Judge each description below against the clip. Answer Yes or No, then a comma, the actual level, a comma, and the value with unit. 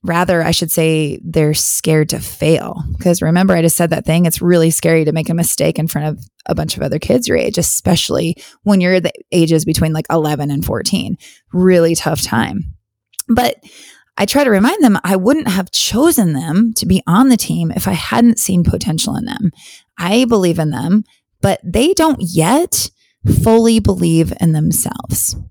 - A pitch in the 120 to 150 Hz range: No, medium, 170 Hz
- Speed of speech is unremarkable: Yes, average, 190 wpm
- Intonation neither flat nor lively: Yes, average, 4.3 semitones